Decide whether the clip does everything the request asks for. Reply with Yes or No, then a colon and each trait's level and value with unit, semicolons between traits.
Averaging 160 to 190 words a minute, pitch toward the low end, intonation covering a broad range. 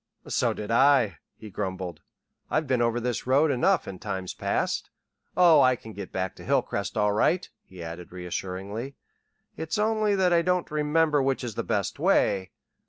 Yes: average, 170 wpm; low, 120 Hz; wide, 7.9 semitones